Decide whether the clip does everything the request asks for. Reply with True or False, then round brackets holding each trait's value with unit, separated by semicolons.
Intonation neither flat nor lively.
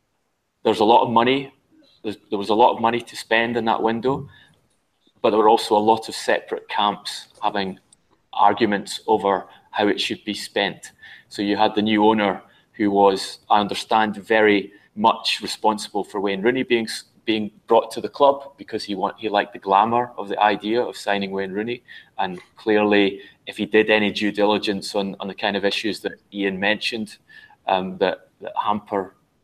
False (2.0 semitones)